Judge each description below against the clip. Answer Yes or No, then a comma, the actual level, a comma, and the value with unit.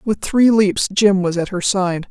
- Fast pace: Yes, fast, 230 wpm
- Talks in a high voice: Yes, high, 195 Hz